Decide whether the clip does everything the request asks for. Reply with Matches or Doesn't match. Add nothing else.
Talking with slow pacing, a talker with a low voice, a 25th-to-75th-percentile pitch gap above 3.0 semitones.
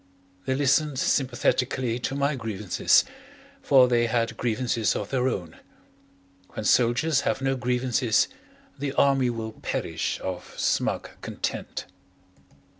Doesn't match